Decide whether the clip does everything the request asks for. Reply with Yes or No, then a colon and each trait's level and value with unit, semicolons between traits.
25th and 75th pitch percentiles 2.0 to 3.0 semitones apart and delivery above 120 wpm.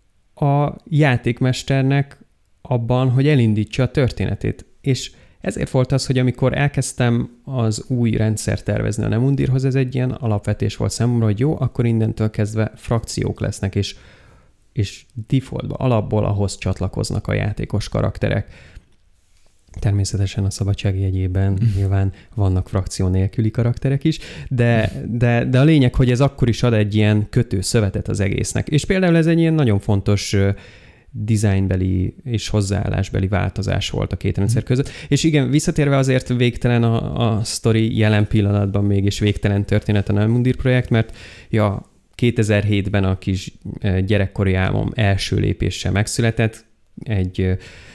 No: average, 4.0 semitones; average, 140 wpm